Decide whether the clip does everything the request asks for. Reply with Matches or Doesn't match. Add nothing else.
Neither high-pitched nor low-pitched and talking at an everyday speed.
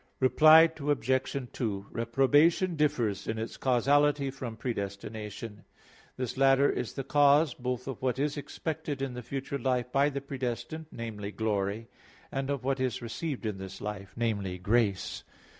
Doesn't match